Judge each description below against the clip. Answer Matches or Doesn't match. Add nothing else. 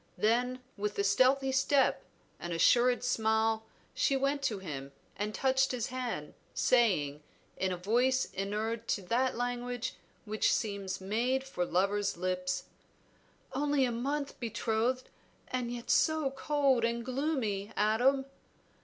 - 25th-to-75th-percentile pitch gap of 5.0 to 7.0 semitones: Doesn't match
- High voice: Matches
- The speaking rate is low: Matches